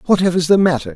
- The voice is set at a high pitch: No, medium, 165 Hz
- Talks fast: No, average, 190 wpm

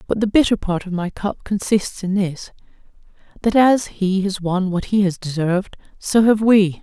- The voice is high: Yes, high, 195 Hz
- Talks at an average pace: Yes, average, 185 wpm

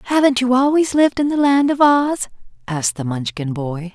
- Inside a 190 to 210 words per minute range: Yes, average, 200 wpm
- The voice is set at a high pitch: Yes, high, 240 Hz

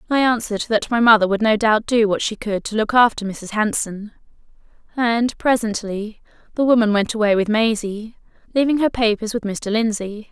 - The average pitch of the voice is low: No, high, 220 Hz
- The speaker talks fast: No, average, 180 wpm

